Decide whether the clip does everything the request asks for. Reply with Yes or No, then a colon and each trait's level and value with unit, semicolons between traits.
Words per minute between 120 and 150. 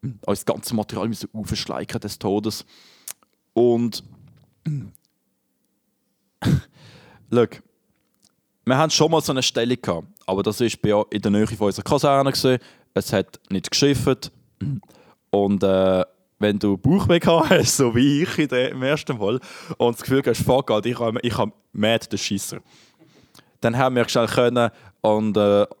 Yes: average, 135 wpm